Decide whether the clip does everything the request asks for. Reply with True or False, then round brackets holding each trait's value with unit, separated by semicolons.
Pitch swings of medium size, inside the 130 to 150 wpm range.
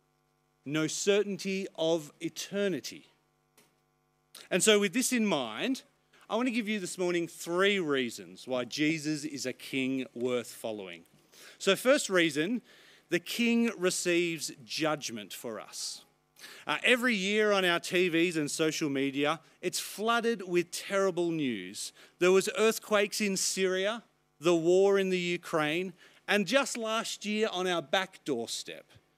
True (4.4 semitones; 140 wpm)